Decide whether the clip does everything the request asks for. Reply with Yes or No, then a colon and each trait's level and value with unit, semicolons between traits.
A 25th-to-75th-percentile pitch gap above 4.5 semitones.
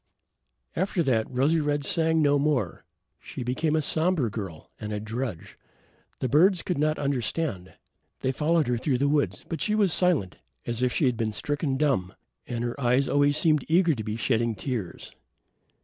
Yes: average, 5.0 semitones